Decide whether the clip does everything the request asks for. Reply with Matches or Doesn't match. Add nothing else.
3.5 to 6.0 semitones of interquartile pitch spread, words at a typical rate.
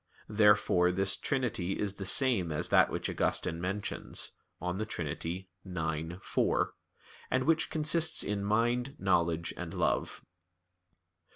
Doesn't match